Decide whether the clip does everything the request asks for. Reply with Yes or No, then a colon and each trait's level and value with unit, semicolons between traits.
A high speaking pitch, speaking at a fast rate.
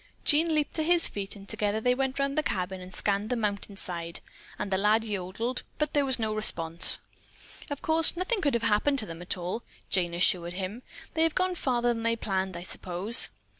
Yes: high, 220 Hz; fast, 210 wpm